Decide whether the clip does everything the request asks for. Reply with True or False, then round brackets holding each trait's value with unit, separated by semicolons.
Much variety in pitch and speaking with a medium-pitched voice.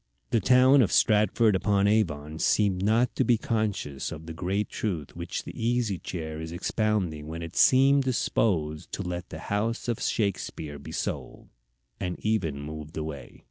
False (5.8 semitones; 100 Hz)